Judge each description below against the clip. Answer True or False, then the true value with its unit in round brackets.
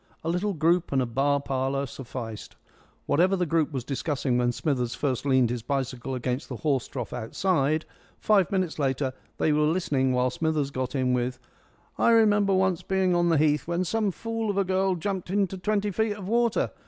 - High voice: False (150 Hz)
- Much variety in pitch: True (6.3 semitones)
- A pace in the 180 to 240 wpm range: True (190 wpm)